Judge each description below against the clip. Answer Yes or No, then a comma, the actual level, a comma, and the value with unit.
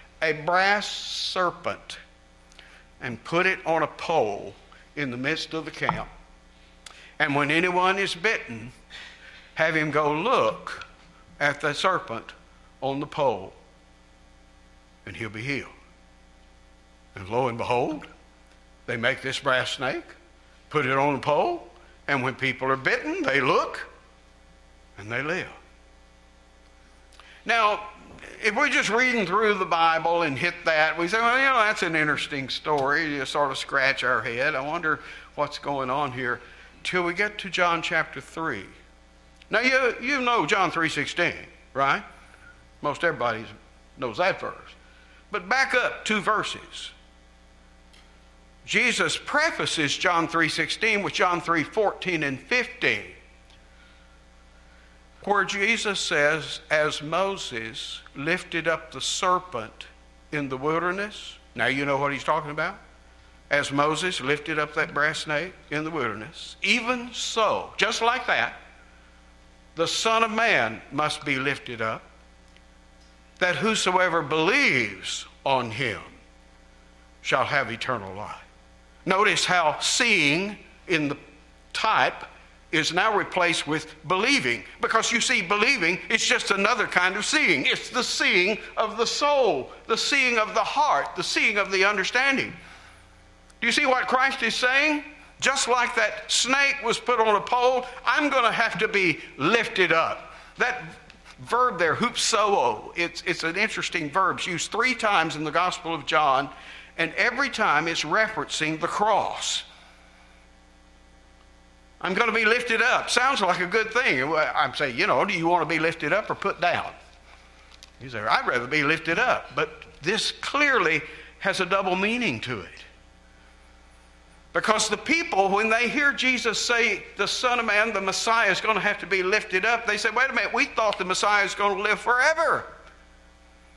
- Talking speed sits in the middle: Yes, average, 150 wpm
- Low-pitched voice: No, medium, 155 Hz